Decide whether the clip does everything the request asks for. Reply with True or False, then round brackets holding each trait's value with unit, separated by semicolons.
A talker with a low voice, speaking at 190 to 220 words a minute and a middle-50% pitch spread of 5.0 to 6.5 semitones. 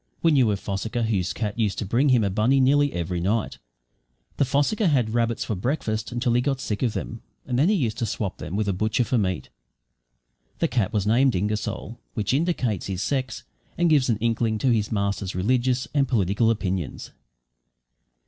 False (115 Hz; 195 wpm; 4.1 semitones)